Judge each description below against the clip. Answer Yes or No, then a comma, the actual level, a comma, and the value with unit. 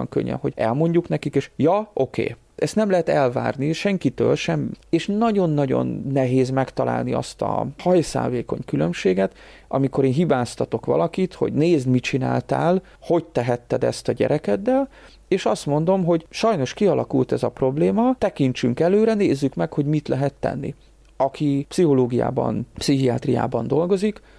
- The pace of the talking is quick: No, average, 140 wpm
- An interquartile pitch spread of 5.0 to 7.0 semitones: Yes, wide, 5.6 semitones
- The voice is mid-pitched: Yes, medium, 145 Hz